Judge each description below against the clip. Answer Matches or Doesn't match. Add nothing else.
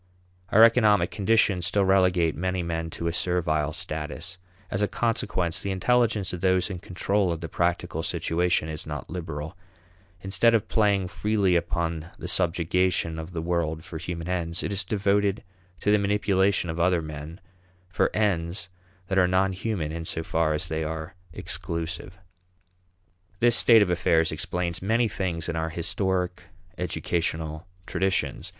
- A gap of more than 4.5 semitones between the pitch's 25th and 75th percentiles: Doesn't match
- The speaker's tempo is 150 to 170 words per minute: Matches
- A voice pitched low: Matches